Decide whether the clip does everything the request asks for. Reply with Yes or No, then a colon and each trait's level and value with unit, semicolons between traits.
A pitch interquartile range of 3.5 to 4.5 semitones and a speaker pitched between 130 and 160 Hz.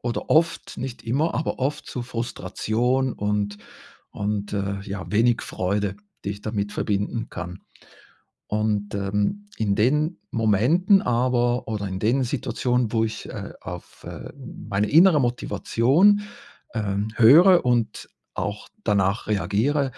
No: average, 4.1 semitones; low, 115 Hz